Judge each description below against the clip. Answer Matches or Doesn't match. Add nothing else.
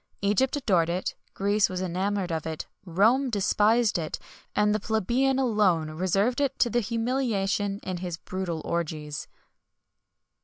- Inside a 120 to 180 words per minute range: Matches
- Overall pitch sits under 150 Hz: Doesn't match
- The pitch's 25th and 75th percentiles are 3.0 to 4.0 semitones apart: Doesn't match